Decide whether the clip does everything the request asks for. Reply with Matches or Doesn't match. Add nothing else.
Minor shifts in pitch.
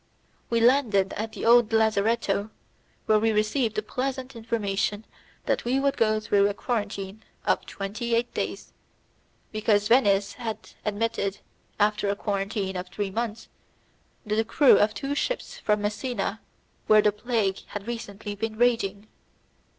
Matches